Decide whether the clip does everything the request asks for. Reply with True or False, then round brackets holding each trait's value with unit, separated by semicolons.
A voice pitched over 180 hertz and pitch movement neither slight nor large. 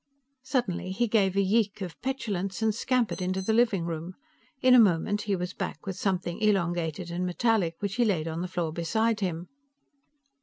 True (190 Hz; 4.0 semitones)